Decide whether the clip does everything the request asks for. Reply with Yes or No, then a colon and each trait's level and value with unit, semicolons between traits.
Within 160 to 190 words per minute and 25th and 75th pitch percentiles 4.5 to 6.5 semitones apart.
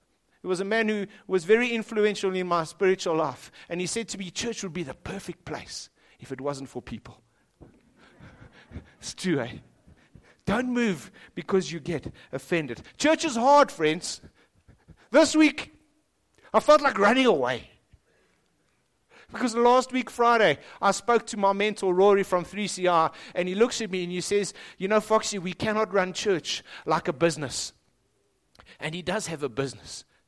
Yes: average, 165 wpm; average, 5.2 semitones